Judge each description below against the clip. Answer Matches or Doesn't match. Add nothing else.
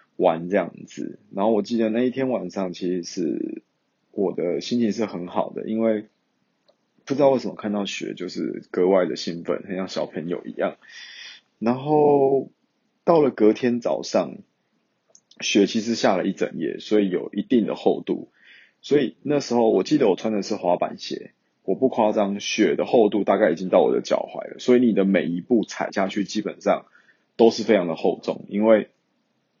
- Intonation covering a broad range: Doesn't match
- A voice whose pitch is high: Doesn't match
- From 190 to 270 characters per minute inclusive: Matches